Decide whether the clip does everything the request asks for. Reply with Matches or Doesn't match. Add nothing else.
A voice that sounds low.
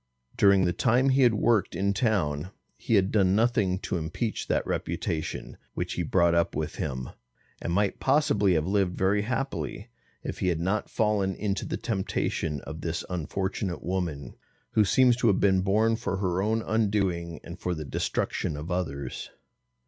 Matches